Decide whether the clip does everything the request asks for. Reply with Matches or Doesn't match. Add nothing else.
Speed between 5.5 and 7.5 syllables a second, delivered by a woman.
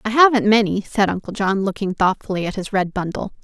Matches